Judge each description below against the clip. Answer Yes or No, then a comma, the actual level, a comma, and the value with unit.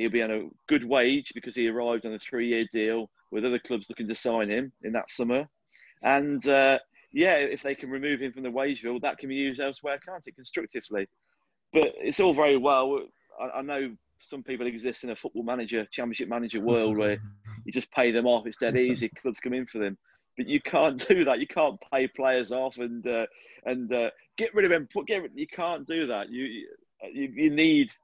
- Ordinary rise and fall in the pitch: Yes, average, 3.7 semitones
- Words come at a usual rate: No, fast, 215 wpm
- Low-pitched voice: Yes, low, 130 Hz